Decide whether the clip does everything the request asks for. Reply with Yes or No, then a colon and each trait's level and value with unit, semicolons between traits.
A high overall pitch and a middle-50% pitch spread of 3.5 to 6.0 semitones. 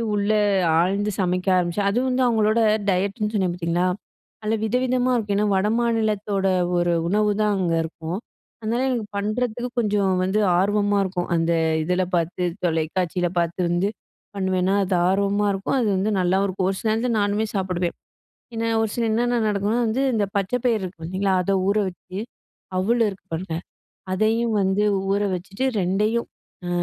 No: high, 200 Hz; average, 3.0 semitones